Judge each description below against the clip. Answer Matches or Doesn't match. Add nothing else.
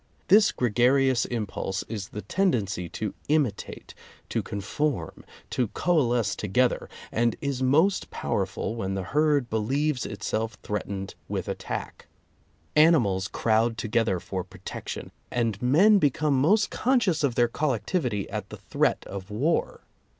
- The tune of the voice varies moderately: Doesn't match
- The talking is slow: Matches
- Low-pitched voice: Matches